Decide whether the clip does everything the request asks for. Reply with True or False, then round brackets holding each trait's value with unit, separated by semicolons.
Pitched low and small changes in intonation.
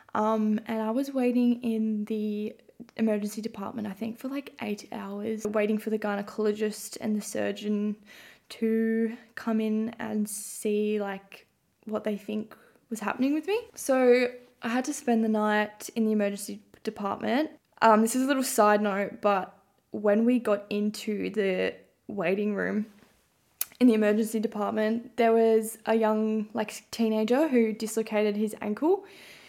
False (220 Hz; 1.4 semitones)